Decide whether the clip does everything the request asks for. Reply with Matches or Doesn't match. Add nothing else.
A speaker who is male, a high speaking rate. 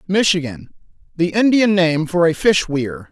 Doesn't match